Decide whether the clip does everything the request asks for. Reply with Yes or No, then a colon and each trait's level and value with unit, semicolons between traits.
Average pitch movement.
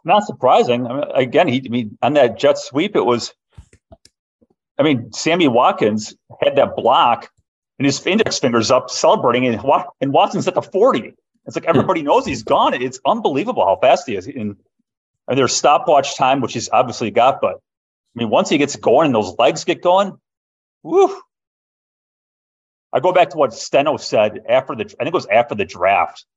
No: wide, 7.2 semitones